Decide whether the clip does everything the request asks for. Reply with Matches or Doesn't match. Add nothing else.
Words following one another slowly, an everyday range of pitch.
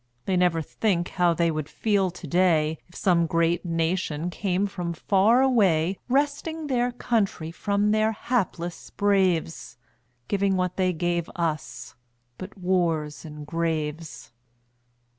Matches